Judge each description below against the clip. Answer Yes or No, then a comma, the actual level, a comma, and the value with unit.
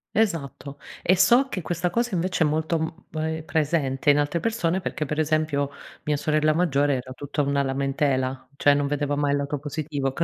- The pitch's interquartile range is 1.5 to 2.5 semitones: No, average, 2.9 semitones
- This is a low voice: No, medium, 150 Hz